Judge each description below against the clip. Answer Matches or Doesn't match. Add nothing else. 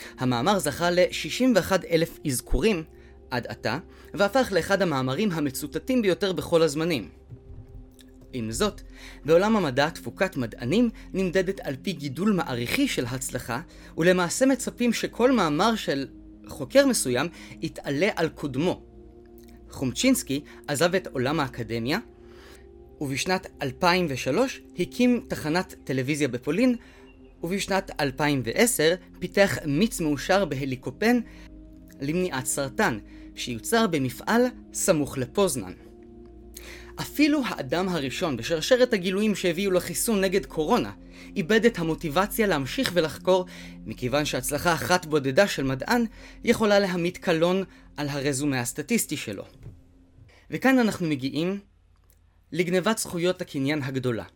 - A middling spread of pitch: Doesn't match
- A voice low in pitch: Doesn't match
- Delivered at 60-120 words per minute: Matches